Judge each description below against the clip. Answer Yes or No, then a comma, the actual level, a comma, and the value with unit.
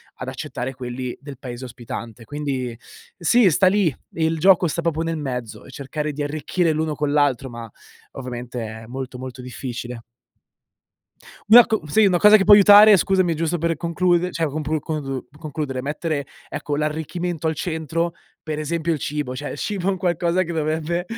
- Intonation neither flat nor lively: Yes, average, 4.5 semitones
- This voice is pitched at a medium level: Yes, medium, 155 Hz